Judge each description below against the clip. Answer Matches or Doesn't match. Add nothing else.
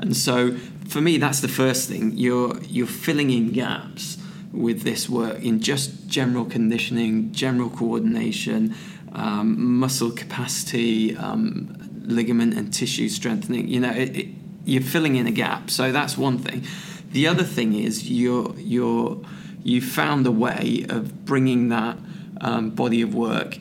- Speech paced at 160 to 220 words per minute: Doesn't match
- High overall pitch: Doesn't match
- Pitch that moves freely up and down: Matches